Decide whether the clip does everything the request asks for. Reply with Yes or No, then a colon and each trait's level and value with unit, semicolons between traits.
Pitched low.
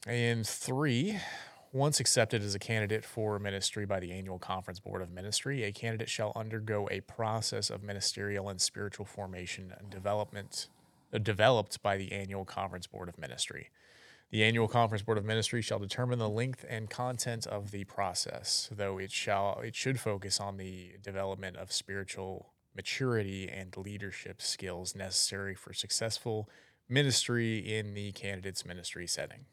Yes: low, 100 Hz